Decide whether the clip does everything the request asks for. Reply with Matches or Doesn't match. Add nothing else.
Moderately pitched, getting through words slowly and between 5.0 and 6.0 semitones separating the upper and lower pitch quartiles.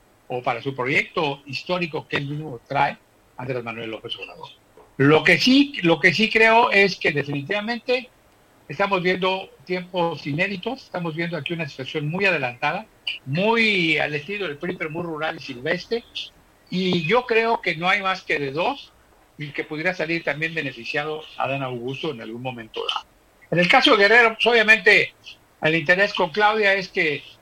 Doesn't match